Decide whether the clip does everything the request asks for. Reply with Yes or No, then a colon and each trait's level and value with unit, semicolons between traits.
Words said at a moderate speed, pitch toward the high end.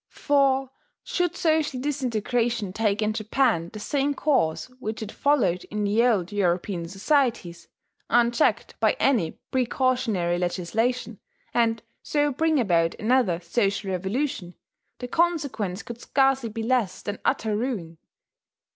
No: slow, 125 wpm; high, 230 Hz